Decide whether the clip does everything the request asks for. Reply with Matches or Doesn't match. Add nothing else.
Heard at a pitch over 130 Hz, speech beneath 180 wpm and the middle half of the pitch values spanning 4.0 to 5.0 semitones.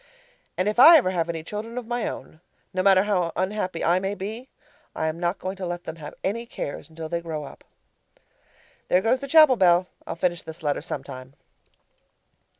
Doesn't match